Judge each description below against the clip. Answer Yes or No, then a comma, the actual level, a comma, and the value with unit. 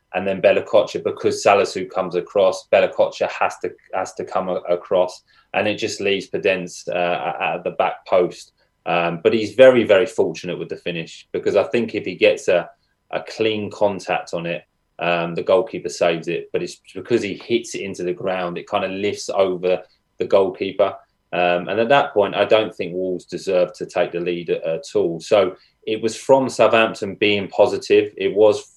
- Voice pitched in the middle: No, low, 110 Hz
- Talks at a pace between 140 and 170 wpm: No, average, 190 wpm